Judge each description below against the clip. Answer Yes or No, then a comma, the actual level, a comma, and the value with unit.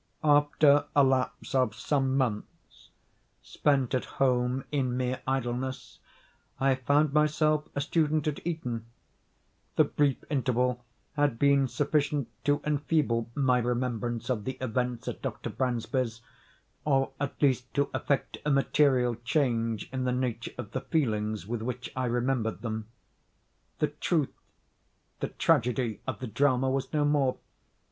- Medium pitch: No, low, 130 Hz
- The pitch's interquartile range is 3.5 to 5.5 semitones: No, average, 2.8 semitones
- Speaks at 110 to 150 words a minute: Yes, slow, 135 wpm